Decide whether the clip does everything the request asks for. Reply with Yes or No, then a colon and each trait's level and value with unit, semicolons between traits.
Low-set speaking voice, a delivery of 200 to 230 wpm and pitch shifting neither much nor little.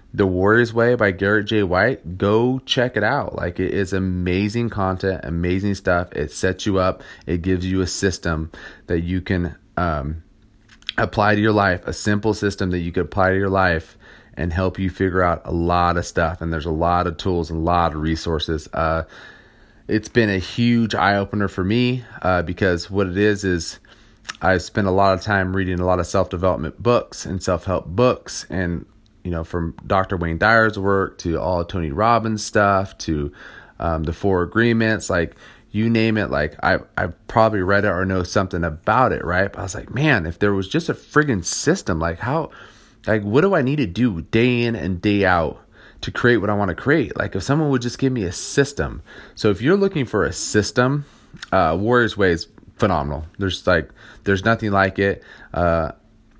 Yes: very low, 95 Hz; fast, 205 wpm; average, 3.7 semitones